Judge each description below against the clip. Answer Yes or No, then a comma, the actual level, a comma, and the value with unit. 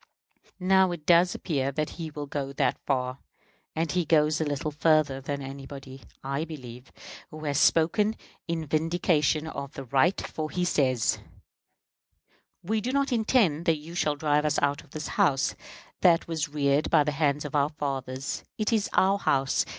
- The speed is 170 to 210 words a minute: Yes, average, 175 wpm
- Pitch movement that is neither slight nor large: Yes, average, 3.2 semitones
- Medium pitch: Yes, medium, 150 Hz